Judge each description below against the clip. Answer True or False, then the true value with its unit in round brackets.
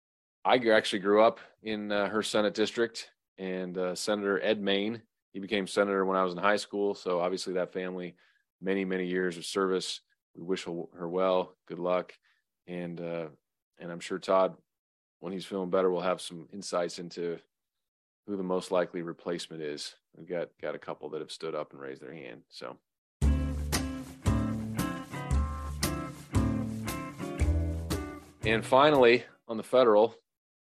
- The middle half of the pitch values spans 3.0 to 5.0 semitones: True (3.6 semitones)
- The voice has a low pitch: True (95 Hz)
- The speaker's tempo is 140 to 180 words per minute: True (150 wpm)